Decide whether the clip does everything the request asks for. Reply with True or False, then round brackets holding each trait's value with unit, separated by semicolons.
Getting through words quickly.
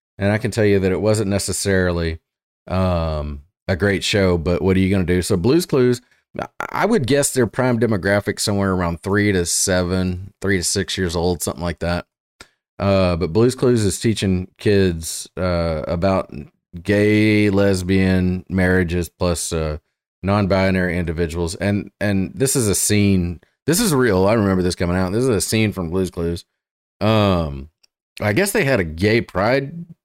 False (175 wpm)